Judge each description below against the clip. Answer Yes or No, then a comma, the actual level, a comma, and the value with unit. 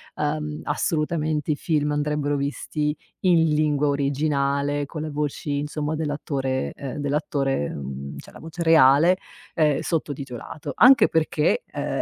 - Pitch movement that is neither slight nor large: No, narrow, 1.6 semitones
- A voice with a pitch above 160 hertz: No, medium, 150 Hz